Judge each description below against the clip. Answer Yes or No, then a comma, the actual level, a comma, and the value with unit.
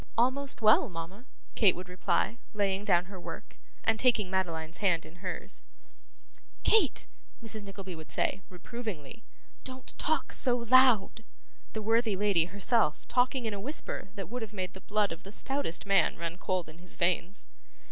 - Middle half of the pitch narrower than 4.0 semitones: No, average, 4.3 semitones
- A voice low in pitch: No, high, 200 Hz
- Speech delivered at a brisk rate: No, average, 165 wpm